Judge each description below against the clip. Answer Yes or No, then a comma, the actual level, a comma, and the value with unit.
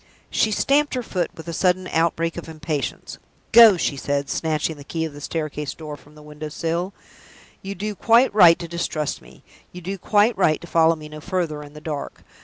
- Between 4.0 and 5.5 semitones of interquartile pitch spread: No, average, 3.5 semitones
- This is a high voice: No, medium, 165 Hz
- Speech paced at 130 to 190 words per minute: No, fast, 205 wpm